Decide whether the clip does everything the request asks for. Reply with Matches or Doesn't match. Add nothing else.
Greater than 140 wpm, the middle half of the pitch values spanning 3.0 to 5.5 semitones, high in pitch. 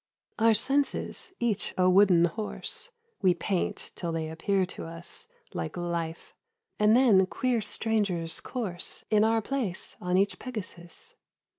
Doesn't match